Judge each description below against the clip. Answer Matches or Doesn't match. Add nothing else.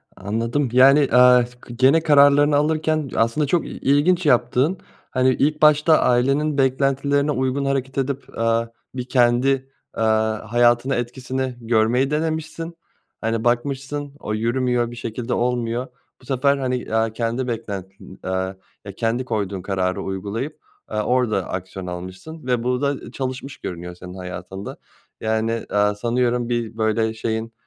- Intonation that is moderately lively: Matches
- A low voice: Matches